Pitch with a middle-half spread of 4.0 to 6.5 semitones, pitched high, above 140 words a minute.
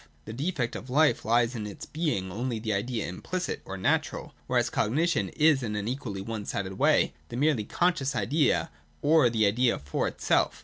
No: wide, 5.5 semitones; low, 120 Hz; average, 180 wpm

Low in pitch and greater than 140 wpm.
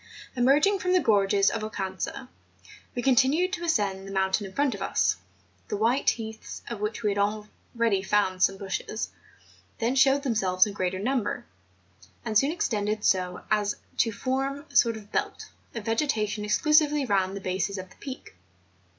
No: high, 215 Hz; average, 170 wpm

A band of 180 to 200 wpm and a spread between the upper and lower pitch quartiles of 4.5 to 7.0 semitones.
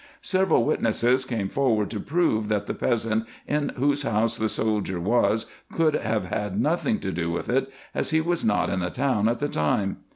Yes: average, 195 wpm; average, 5.2 semitones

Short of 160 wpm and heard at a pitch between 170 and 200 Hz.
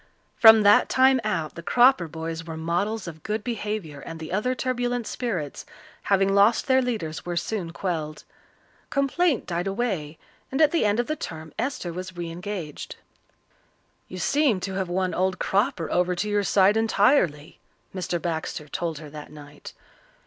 No: average, 165 wpm; high, 190 Hz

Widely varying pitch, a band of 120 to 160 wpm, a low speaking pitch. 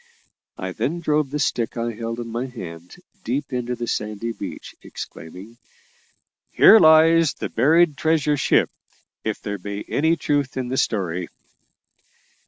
Yes: wide, 5.7 semitones; average, 145 wpm; low, 120 Hz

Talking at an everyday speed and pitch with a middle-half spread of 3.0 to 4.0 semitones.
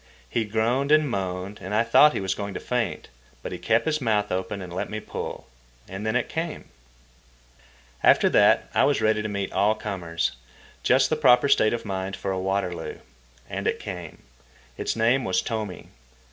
Yes: average, 185 wpm; average, 3.6 semitones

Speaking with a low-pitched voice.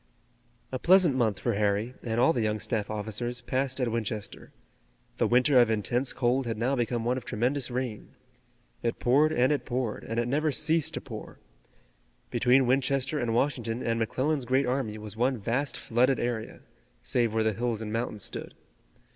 Yes: low, 120 Hz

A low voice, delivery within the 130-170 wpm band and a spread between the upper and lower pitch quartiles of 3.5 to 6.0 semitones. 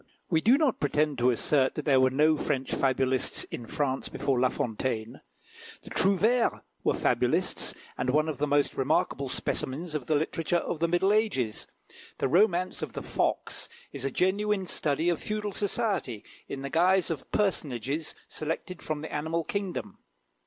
No: medium, 155 Hz; average, 165 wpm; wide, 5.5 semitones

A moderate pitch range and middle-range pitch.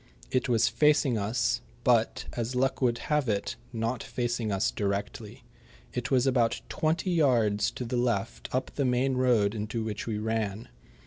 No: average, 3.3 semitones; low, 120 Hz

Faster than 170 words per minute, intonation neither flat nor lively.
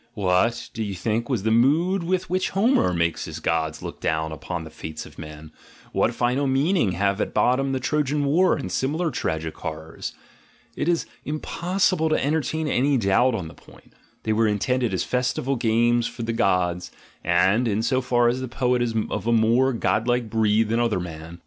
No: average, 190 wpm; wide, 6.2 semitones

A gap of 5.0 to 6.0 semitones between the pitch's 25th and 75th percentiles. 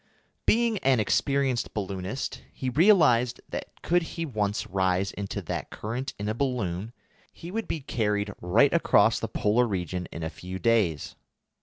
Yes: wide, 5.6 semitones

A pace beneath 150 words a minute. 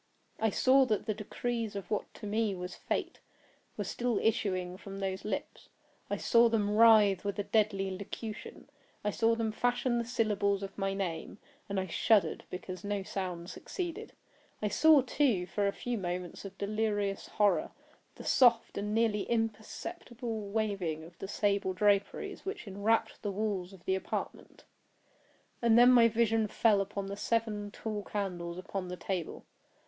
No: average, 165 wpm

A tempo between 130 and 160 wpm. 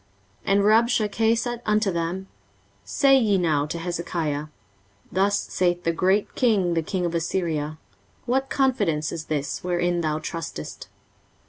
Yes: average, 140 wpm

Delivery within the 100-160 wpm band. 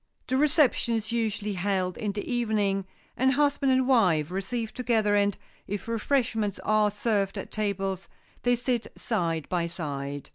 Yes: average, 150 wpm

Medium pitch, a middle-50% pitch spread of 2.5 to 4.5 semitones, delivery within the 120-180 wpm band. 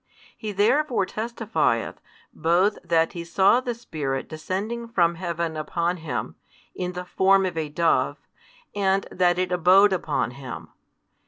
Yes: medium, 180 Hz; average, 3.6 semitones; average, 140 wpm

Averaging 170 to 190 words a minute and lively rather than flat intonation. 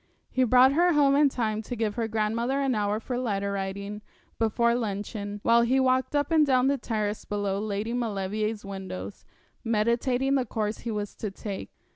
No: average, 180 wpm; average, 3.6 semitones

